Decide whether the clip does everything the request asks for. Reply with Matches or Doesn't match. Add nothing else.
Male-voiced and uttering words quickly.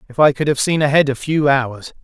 Matches